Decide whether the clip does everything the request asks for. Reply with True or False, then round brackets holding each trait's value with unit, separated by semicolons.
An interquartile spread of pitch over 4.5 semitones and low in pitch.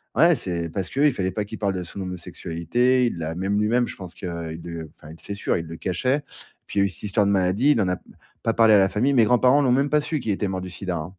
True (5.3 semitones; 100 Hz)